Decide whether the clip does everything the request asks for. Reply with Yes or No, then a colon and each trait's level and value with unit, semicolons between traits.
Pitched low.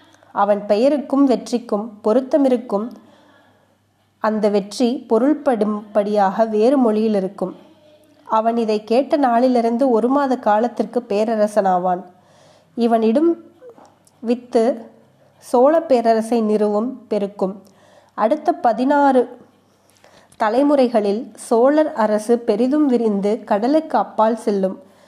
No: high, 230 Hz